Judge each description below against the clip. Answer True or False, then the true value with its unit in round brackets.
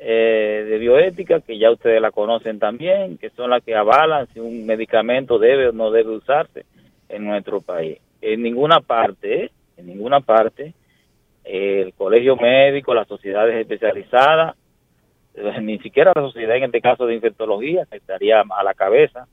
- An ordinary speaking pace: True (160 wpm)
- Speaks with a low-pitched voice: True (115 Hz)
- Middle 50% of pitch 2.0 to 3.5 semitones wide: False (4.3 semitones)